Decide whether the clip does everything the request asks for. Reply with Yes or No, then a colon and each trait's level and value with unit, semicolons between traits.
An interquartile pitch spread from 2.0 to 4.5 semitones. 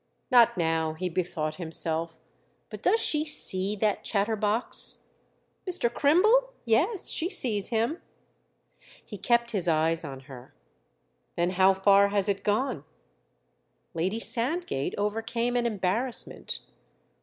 No: average, 5.3 semitones